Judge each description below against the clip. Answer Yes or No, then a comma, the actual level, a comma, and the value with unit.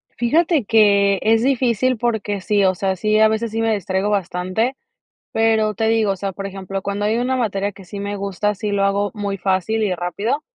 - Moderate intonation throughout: No, narrow, 2.2 semitones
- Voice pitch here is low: No, high, 205 Hz